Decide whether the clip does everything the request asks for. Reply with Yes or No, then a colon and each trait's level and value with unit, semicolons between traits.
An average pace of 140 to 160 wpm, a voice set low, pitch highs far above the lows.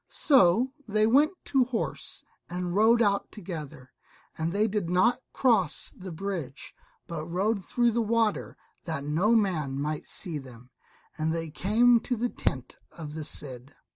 No: average, 155 wpm; medium, 185 Hz; wide, 6.5 semitones